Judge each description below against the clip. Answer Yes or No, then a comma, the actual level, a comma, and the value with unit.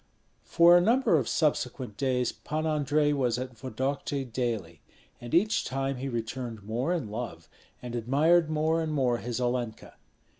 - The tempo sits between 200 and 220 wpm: No, average, 155 wpm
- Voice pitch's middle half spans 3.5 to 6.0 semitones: Yes, average, 4.3 semitones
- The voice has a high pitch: No, low, 130 Hz